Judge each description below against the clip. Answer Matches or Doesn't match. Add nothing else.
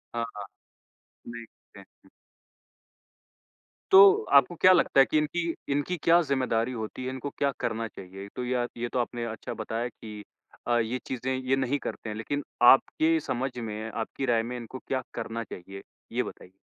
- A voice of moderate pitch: Doesn't match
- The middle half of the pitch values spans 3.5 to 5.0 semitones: Doesn't match